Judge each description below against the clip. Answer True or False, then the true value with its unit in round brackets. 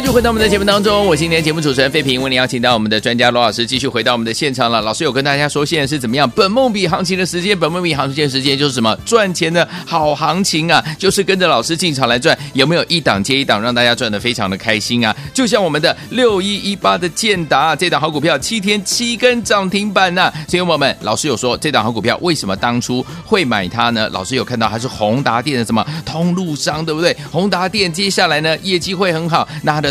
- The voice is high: False (155 Hz)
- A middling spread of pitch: False (6.9 semitones)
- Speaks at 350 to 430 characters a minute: True (385 characters per minute)